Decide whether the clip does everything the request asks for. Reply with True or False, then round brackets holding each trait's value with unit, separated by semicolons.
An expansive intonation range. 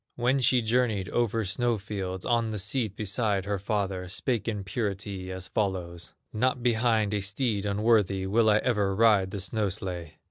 False (3.1 semitones)